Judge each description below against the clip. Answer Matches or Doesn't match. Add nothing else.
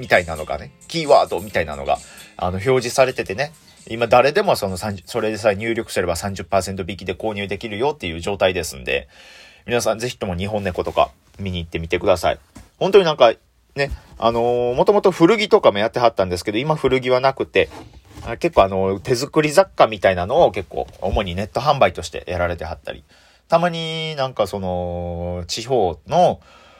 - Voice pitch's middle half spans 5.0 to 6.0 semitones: Matches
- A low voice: Matches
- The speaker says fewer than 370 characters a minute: Doesn't match